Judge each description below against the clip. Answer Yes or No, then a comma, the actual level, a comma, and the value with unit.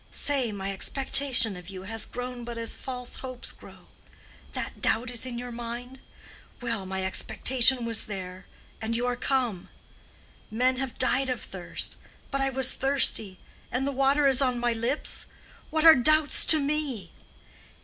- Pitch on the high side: Yes, high, 245 Hz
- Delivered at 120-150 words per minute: No, average, 160 wpm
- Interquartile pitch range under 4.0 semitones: Yes, average, 2.9 semitones